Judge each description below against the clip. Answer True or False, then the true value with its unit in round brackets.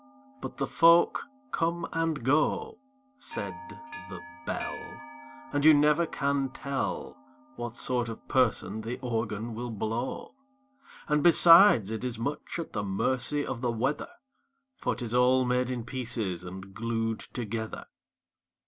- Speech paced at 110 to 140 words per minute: True (135 wpm)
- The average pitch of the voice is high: False (125 Hz)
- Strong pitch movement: False (4.5 semitones)